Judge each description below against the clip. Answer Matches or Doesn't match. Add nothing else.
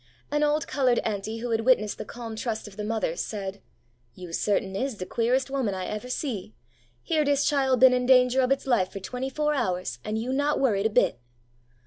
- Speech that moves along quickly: Matches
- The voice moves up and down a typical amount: Matches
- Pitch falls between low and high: Doesn't match